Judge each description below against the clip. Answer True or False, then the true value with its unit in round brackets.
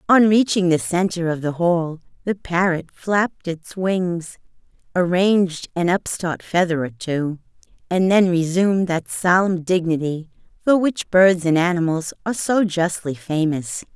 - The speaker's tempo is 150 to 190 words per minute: False (140 wpm)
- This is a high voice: False (175 Hz)